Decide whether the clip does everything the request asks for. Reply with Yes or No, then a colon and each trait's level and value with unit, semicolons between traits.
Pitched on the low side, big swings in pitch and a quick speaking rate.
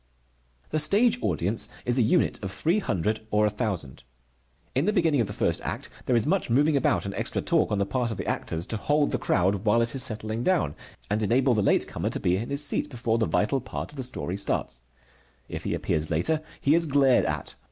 Yes: low, 115 Hz; wide, 5.7 semitones; fast, 230 wpm